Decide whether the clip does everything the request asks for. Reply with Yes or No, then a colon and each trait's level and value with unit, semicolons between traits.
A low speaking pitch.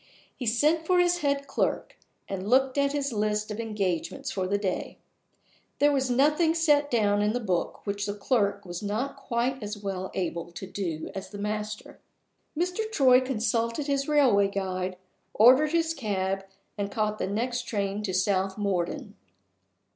No: high, 215 Hz